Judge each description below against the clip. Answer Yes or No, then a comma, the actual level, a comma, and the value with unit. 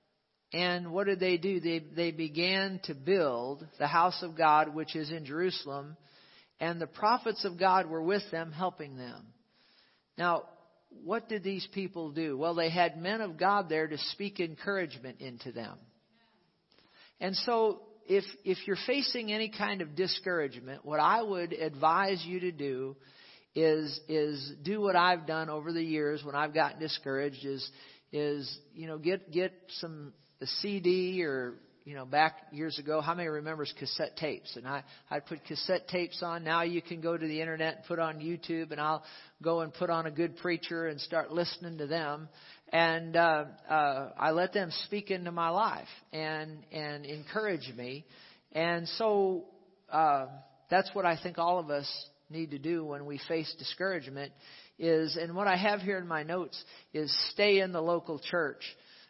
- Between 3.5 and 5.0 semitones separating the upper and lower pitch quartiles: No, average, 3.1 semitones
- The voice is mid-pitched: Yes, medium, 165 Hz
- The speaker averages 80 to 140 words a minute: No, average, 175 wpm